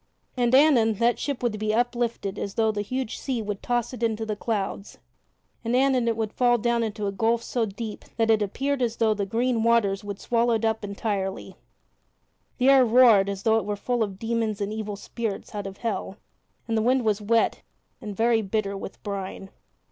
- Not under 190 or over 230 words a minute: Yes, fast, 205 wpm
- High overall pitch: Yes, high, 225 Hz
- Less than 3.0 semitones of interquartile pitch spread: Yes, narrow, 2.5 semitones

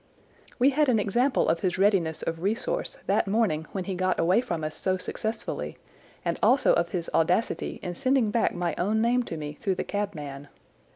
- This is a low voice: No, high, 195 Hz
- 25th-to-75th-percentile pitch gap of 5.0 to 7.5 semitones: Yes, average, 5.3 semitones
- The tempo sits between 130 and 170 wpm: No, average, 190 wpm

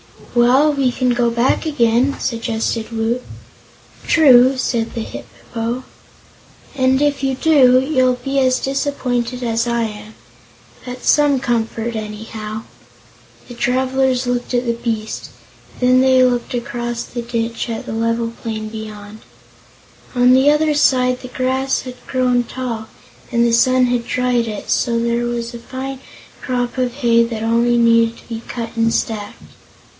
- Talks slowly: No, average, 155 wpm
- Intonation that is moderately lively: No, narrow, 1.9 semitones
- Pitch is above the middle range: Yes, high, 240 Hz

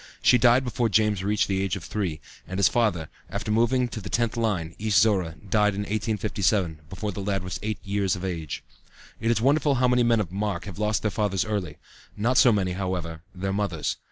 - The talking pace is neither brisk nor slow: No, fast, 210 wpm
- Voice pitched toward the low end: Yes, low, 105 Hz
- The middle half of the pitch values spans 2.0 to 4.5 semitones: Yes, average, 3.1 semitones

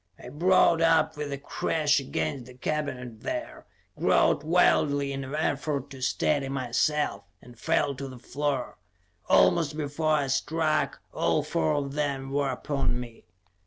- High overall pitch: No, medium, 140 Hz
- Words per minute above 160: No, average, 150 wpm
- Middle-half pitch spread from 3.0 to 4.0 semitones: No, narrow, 2.5 semitones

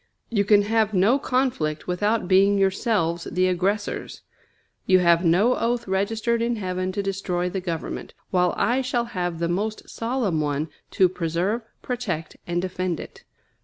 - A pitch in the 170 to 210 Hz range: Yes, high, 190 Hz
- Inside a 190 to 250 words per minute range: No, average, 155 wpm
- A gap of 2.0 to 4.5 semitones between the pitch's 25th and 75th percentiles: Yes, average, 4.0 semitones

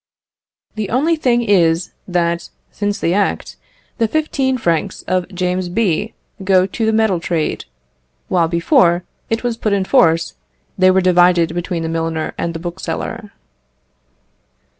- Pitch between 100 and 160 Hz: No, medium, 185 Hz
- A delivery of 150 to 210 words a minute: No, average, 140 wpm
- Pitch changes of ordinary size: Yes, average, 4.4 semitones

